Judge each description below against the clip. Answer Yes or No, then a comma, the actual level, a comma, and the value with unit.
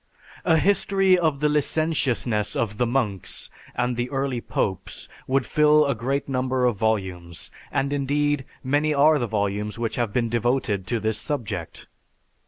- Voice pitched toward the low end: Yes, low, 125 Hz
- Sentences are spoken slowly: No, average, 155 wpm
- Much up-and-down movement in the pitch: No, average, 4.9 semitones